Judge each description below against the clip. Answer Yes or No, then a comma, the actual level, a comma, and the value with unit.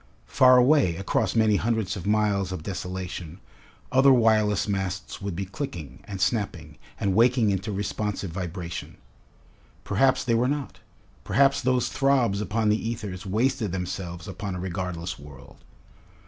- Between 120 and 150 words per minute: Yes, average, 140 wpm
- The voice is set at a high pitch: No, low, 100 Hz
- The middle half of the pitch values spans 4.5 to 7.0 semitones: No, average, 4.0 semitones